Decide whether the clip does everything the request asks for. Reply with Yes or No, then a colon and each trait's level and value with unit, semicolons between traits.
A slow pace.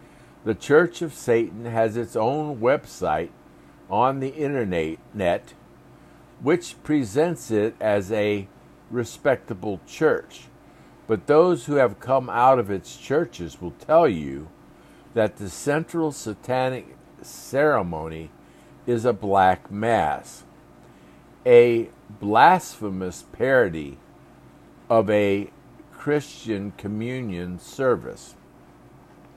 Yes: slow, 95 wpm